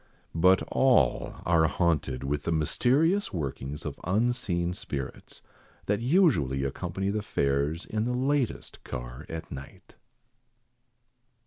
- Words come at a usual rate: No, slow, 115 wpm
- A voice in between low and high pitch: No, very low, 85 Hz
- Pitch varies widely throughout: Yes, wide, 8.4 semitones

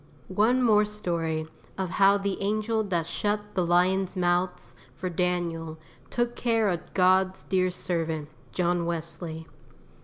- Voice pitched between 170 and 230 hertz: Yes, medium, 185 Hz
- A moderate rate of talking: No, slow, 130 wpm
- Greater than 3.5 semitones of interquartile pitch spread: No, average, 3.2 semitones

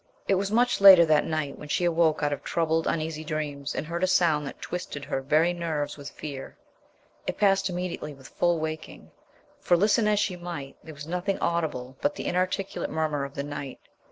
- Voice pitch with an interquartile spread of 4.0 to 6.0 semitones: No, average, 3.5 semitones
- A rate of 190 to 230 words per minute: Yes, average, 200 wpm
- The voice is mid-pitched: Yes, medium, 160 Hz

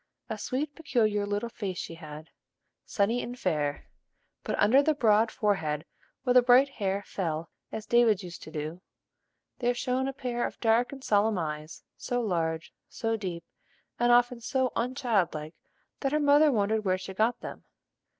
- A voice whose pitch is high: Yes, high, 220 Hz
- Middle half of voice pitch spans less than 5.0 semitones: No, average, 5.3 semitones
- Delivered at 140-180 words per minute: Yes, average, 165 wpm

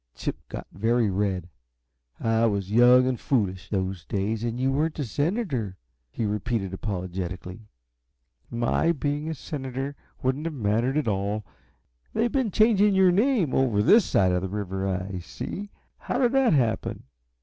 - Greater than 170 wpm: No, average, 150 wpm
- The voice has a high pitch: No, low, 115 Hz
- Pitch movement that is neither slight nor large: No, wide, 7.3 semitones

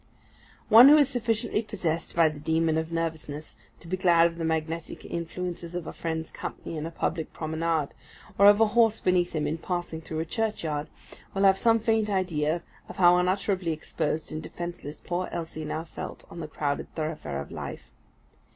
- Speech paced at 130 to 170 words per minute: No, average, 185 wpm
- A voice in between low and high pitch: Yes, medium, 165 Hz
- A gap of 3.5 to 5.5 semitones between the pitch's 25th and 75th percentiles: No, average, 2.9 semitones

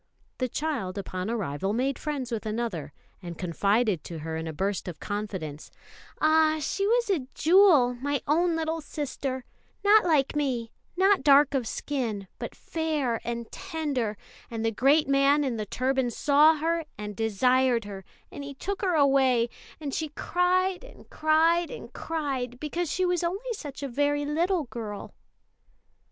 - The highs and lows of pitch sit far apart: Yes, wide, 5.9 semitones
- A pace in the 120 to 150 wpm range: No, average, 160 wpm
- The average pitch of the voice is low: No, very high, 275 Hz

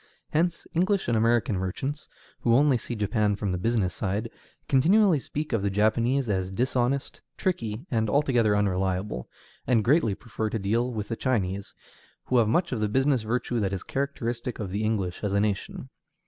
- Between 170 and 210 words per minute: Yes, average, 175 wpm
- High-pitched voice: No, low, 115 Hz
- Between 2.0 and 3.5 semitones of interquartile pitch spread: No, average, 4.2 semitones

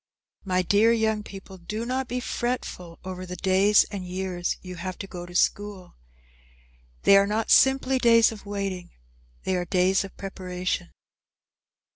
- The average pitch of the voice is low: No, high, 195 Hz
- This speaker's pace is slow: No, average, 155 wpm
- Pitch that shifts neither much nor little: Yes, average, 3.0 semitones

